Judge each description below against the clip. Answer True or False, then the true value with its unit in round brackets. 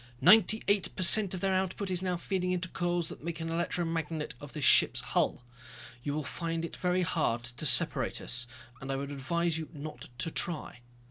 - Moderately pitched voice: True (165 Hz)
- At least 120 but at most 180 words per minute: False (200 wpm)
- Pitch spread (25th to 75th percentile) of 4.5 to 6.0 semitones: False (3.8 semitones)